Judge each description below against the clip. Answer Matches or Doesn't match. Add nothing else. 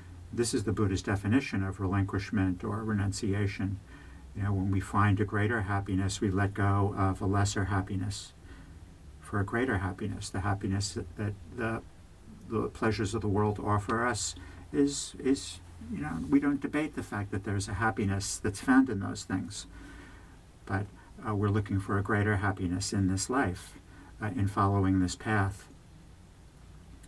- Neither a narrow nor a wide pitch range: Doesn't match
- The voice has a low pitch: Matches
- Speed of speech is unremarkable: Matches